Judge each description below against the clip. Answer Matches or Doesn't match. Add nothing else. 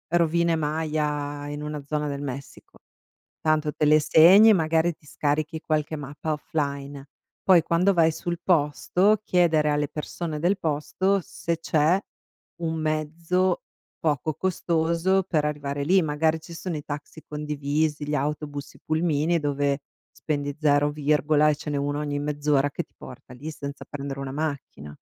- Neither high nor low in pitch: Matches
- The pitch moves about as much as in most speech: Doesn't match